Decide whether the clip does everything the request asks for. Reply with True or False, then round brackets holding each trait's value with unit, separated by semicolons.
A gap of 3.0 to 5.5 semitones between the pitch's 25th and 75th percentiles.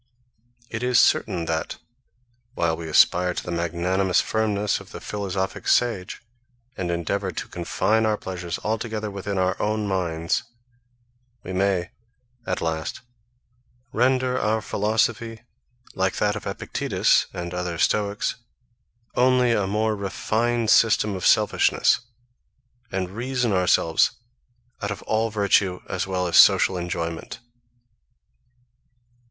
True (3.4 semitones)